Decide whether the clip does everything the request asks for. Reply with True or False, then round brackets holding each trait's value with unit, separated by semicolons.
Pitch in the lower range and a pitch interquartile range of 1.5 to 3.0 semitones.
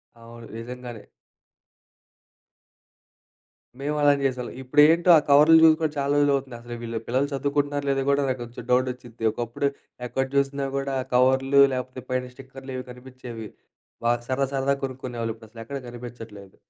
True (130 Hz; 2.6 semitones)